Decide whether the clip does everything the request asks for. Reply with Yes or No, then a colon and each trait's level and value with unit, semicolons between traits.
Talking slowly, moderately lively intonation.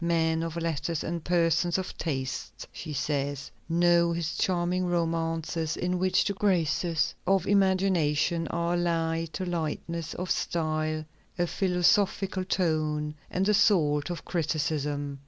No: slow, 130 wpm; narrow, 2.2 semitones